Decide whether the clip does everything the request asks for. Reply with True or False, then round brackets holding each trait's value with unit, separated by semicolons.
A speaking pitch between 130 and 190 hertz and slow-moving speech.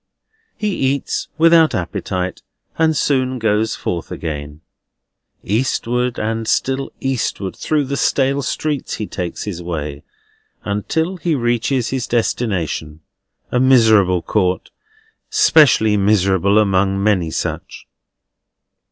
False (110 Hz; 110 wpm)